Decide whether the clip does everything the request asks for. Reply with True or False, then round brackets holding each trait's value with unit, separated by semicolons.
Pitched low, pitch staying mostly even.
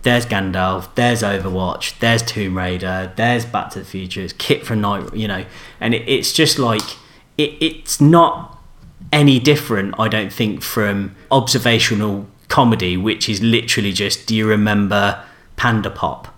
False (110 Hz; 3.5 semitones)